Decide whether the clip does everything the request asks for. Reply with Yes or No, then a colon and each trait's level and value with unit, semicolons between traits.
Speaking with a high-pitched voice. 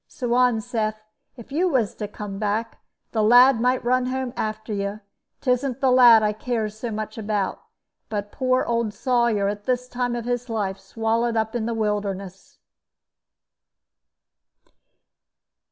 Yes: high, 225 Hz